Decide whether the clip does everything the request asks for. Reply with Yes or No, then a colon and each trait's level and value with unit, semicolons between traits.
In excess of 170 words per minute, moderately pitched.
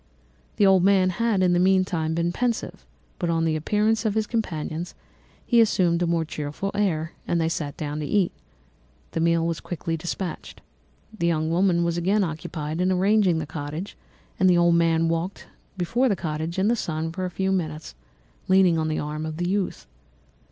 Yes: average, 185 wpm; medium, 170 Hz